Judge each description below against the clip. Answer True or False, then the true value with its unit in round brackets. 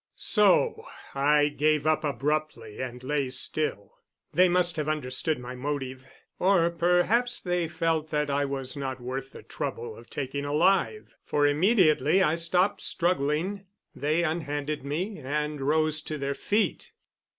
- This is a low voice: False (150 Hz)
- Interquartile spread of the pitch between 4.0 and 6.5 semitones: False (3.6 semitones)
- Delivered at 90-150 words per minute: True (140 wpm)